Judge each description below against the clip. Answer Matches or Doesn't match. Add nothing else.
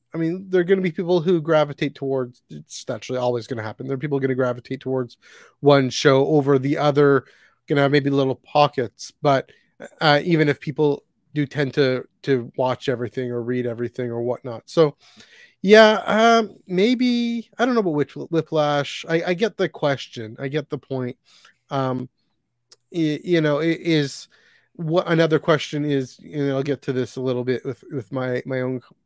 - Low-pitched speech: Doesn't match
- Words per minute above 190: Matches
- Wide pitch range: Doesn't match